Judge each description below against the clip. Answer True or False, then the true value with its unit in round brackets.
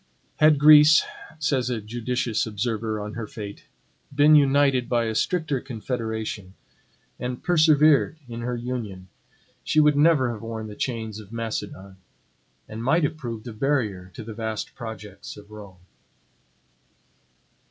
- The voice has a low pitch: True (115 Hz)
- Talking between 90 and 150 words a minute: True (140 wpm)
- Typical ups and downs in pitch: True (4.5 semitones)